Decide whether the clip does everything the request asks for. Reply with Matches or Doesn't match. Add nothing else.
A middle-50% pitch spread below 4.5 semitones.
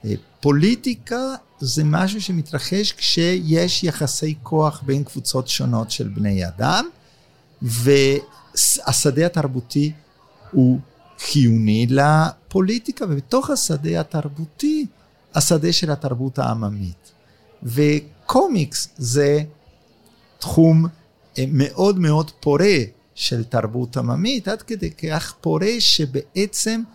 Doesn't match